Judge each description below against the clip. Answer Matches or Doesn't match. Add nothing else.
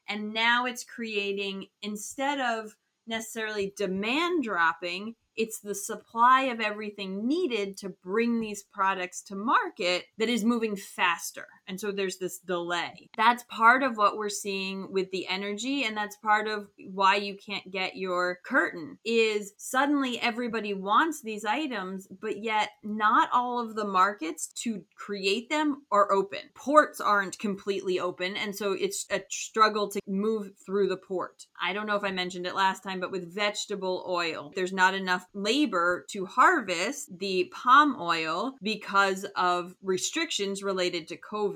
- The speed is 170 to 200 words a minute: Doesn't match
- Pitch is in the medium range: Doesn't match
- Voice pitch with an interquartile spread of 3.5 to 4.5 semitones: Doesn't match